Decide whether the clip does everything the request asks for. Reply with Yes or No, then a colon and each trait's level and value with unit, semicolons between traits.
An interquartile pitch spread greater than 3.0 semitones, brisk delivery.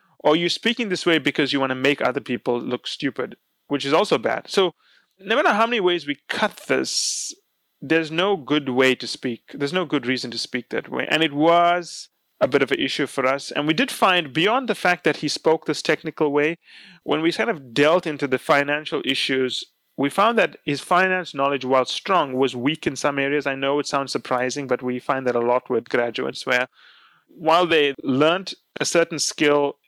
Yes: average, 3.8 semitones; fast, 215 wpm